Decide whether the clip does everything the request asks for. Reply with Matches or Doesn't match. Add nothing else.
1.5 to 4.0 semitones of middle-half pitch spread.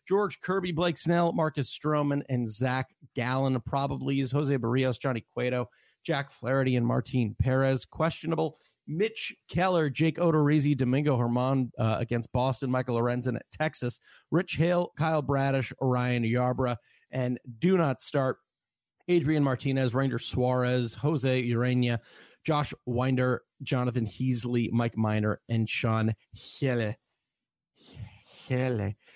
Matches